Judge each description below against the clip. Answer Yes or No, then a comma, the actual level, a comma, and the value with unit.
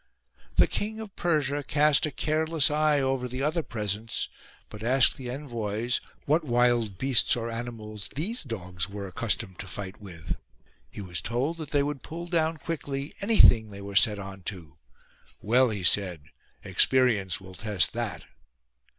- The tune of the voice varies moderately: No, wide, 6.5 semitones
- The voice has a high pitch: No, low, 120 Hz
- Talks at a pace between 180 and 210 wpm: No, average, 160 wpm